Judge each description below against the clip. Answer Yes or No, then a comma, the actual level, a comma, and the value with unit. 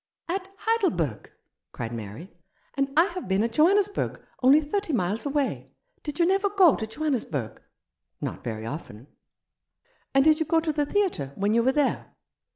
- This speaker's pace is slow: No, average, 170 wpm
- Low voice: No, very high, 280 Hz